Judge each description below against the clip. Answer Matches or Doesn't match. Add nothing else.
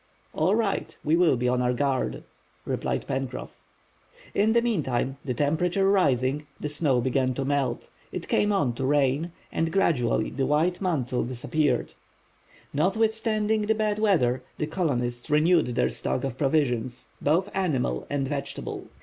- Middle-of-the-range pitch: Matches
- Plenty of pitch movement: Matches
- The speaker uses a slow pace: Doesn't match